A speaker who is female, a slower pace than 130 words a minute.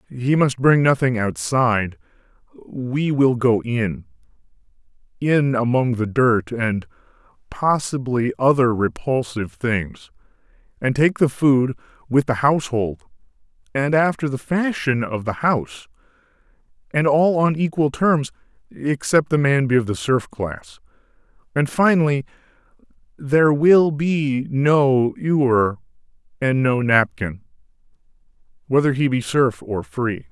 No: male; slow, 115 wpm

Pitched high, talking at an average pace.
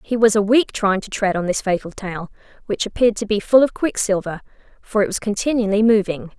No: high, 210 Hz; fast, 215 wpm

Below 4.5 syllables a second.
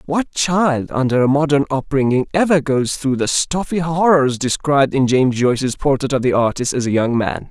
No: 5.1 syllables/s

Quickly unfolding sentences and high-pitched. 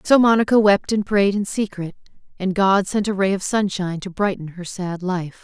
Yes: fast, 210 wpm; high, 195 Hz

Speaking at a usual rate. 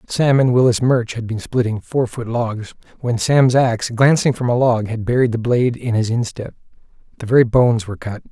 No: fast, 210 wpm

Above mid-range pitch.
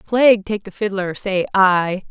Yes: high, 200 Hz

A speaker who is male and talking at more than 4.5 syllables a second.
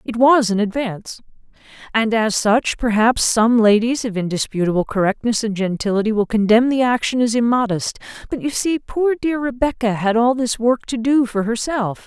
No: female; 5.0 syllables/s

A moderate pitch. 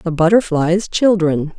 Yes: medium, 175 Hz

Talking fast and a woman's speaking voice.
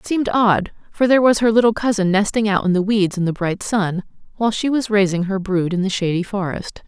Yes: fast, 245 wpm; female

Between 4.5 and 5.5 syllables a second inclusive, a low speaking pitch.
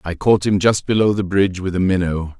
No: 5.7 syllables/s; very low, 95 Hz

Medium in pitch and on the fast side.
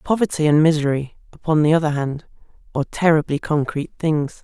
No: medium, 155 Hz; average, 150 wpm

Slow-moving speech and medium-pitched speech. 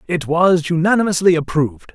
Yes: slow, 125 wpm; medium, 165 Hz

